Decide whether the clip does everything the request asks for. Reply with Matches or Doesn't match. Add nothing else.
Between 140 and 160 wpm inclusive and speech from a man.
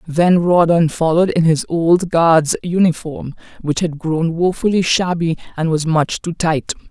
Doesn't match